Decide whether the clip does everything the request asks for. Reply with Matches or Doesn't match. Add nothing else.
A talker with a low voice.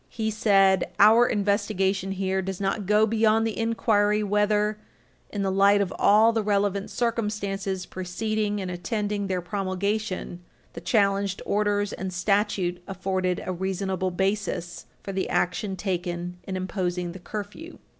Doesn't match